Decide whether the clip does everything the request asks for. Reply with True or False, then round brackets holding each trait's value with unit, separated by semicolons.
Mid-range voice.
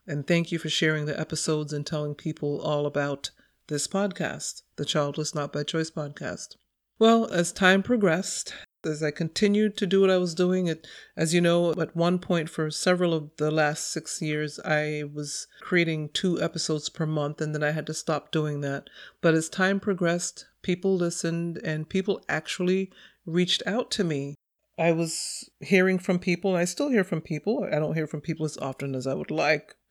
True (160 Hz)